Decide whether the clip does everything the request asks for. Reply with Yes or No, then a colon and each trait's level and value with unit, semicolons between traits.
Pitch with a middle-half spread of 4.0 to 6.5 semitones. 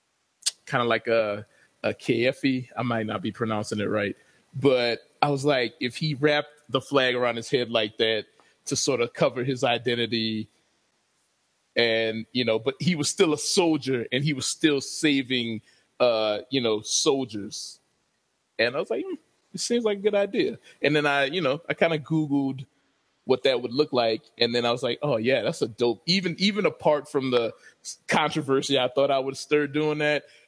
Yes: average, 4.3 semitones